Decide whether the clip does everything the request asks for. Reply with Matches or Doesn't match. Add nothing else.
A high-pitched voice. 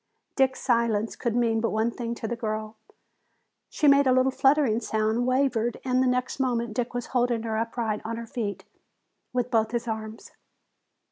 Matches